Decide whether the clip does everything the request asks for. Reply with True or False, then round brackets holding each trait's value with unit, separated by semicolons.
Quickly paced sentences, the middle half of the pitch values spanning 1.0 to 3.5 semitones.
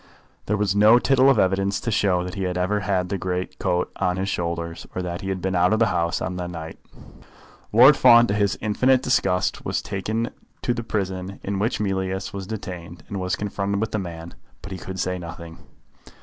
True (215 wpm; 2.5 semitones)